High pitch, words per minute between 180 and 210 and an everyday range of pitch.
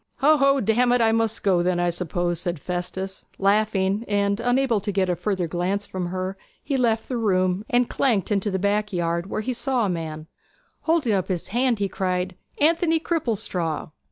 Yes: high, 200 Hz; average, 190 wpm; average, 4.5 semitones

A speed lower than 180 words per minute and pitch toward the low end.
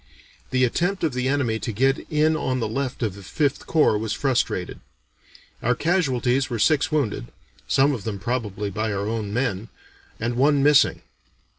Yes: average, 170 wpm; low, 125 Hz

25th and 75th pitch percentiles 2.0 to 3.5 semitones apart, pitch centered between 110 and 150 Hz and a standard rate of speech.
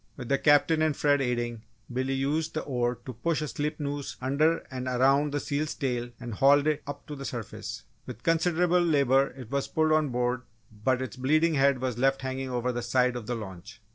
No: average, 3.1 semitones; low, 135 Hz; fast, 210 wpm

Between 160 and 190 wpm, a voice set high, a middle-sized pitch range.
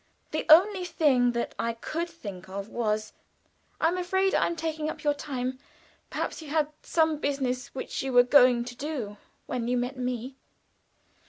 Yes: average, 170 wpm; very high, 265 Hz; average, 4.5 semitones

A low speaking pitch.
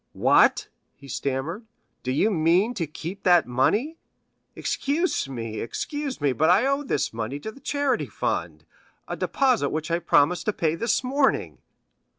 No: medium, 175 Hz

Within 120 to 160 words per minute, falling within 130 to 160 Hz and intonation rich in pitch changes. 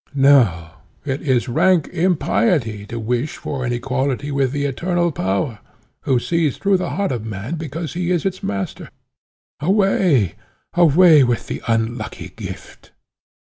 Yes: average, 140 wpm; medium, 140 Hz; wide, 6.1 semitones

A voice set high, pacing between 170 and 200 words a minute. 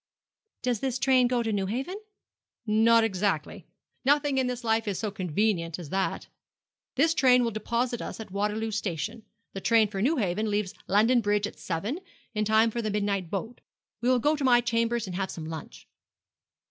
Yes: high, 220 Hz; average, 180 wpm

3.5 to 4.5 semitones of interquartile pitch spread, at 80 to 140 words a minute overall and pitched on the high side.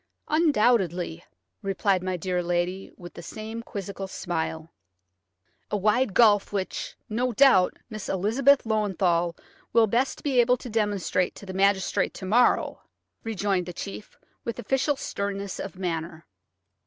Yes: average, 3.9 semitones; slow, 135 wpm; high, 200 Hz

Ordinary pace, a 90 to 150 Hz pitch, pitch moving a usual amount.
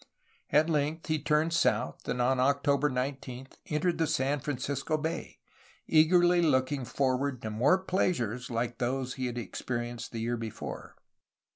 Yes: average, 145 wpm; low, 135 Hz; average, 3.9 semitones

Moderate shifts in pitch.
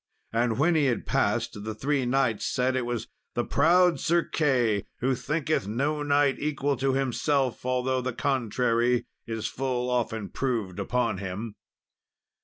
Yes: average, 3.4 semitones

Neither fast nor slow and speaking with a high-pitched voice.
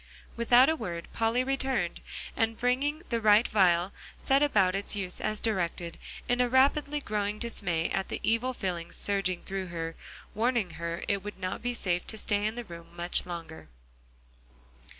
Yes: average, 170 wpm; high, 205 Hz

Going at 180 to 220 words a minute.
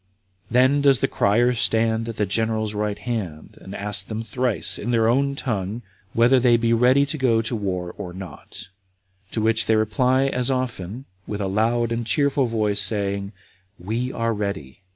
Yes: average, 185 wpm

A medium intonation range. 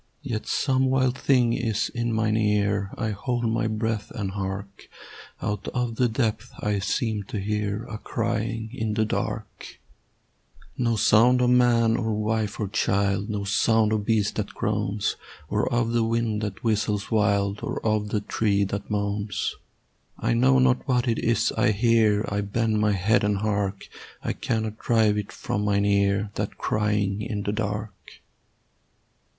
No: narrow, 2.1 semitones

